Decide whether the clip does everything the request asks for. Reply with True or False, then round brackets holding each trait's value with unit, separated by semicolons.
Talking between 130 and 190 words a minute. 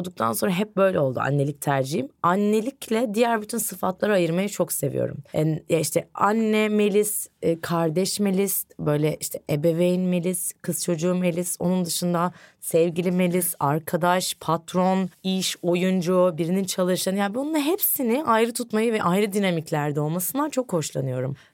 True (135 wpm)